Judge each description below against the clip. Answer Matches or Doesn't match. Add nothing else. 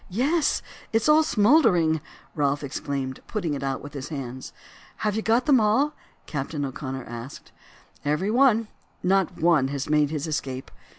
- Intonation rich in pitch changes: Matches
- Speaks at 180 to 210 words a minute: Doesn't match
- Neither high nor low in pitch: Matches